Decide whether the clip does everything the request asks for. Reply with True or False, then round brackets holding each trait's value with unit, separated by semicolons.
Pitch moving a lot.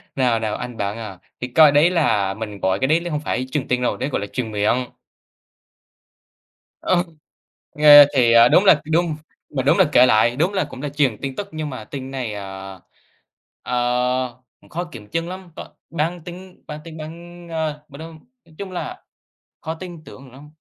True (5.7 semitones)